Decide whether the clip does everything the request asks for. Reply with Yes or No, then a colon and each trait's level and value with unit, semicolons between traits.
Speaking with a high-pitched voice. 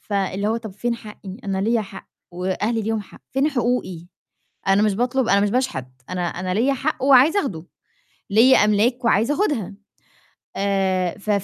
Yes: high, 215 Hz